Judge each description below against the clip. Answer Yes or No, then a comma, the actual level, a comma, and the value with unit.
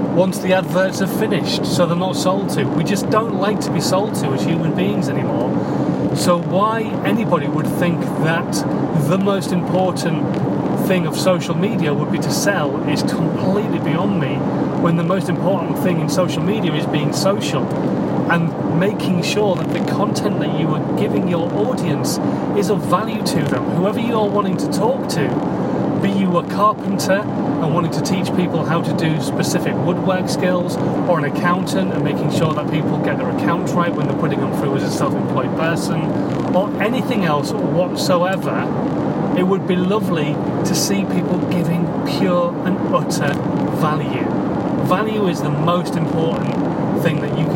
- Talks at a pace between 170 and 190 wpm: Yes, average, 175 wpm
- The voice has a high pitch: No, medium, 180 Hz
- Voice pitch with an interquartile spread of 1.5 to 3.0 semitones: Yes, narrow, 2.6 semitones